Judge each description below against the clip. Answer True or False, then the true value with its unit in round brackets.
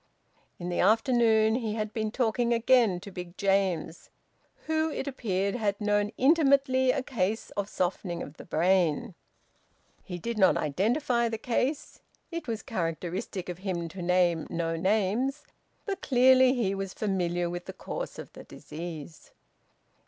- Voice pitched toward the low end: False (205 Hz)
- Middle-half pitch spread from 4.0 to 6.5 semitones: True (5.3 semitones)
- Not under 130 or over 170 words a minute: True (150 wpm)